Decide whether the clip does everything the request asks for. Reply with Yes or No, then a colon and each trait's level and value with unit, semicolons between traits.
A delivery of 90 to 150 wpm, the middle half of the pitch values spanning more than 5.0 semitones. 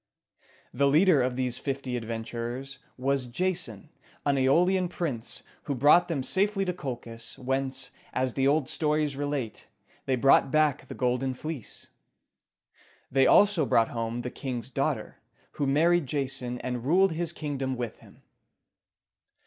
No: average, 140 wpm; average, 3.7 semitones